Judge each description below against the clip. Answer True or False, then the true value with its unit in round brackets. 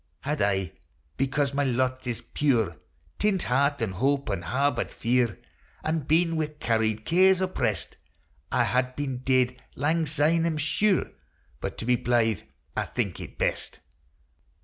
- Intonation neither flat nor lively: True (4.5 semitones)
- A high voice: False (130 Hz)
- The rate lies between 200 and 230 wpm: False (150 wpm)